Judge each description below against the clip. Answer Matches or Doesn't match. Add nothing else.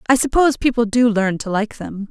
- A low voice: Doesn't match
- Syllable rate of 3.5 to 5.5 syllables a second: Doesn't match